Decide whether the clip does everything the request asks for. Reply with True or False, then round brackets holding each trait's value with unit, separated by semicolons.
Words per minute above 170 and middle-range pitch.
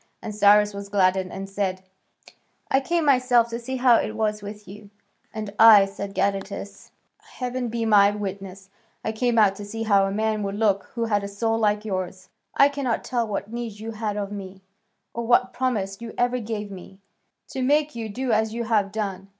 False (200 wpm; 210 Hz)